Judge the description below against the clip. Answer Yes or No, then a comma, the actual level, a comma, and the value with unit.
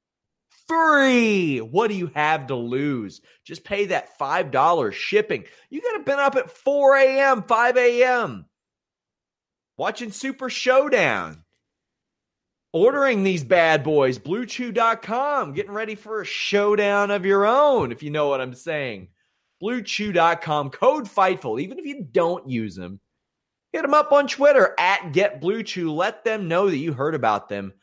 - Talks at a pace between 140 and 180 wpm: Yes, average, 145 wpm